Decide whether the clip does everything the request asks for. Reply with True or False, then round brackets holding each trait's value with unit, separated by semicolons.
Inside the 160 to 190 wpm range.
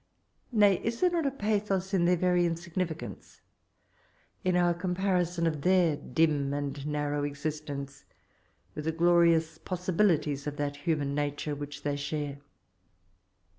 False (135 wpm)